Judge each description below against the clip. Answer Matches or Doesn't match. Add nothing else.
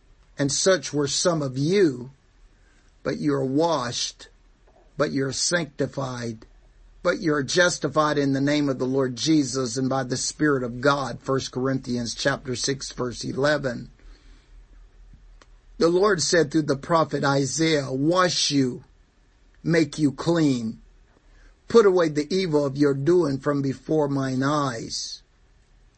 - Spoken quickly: Doesn't match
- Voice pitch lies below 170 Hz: Matches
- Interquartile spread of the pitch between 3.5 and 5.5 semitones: Doesn't match